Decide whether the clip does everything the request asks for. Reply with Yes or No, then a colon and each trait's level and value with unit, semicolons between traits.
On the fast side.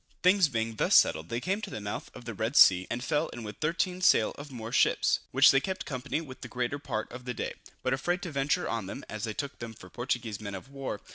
Yes: fast, 260 wpm